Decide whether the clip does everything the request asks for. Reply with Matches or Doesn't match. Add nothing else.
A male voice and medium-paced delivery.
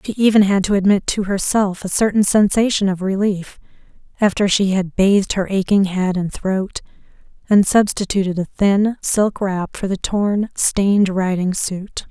Doesn't match